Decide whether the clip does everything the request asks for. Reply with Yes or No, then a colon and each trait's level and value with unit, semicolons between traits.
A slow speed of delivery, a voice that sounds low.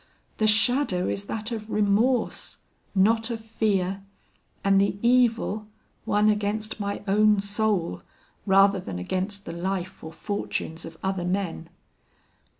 No: slow, 130 wpm; high, 200 Hz